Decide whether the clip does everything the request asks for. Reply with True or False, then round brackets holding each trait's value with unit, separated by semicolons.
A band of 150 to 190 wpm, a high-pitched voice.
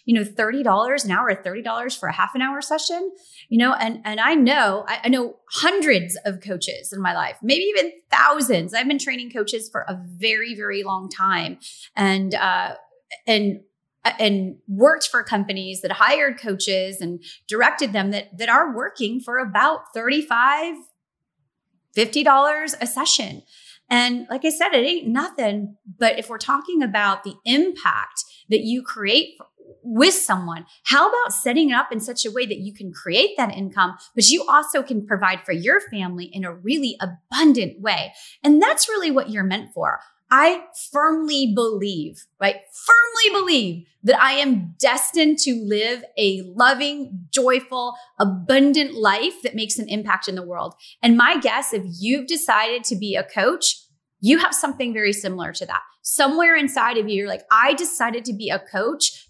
True (170 wpm; 235 Hz)